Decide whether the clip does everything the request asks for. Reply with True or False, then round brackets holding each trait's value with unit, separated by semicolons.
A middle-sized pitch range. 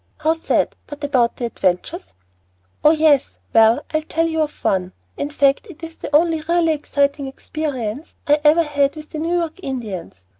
True (3.6 semitones)